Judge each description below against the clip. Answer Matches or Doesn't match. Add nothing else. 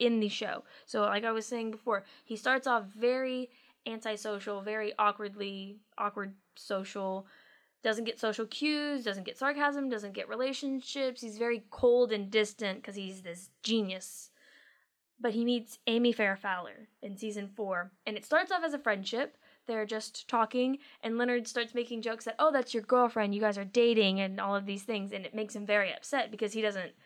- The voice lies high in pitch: Matches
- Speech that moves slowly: Doesn't match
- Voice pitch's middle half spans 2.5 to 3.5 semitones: Matches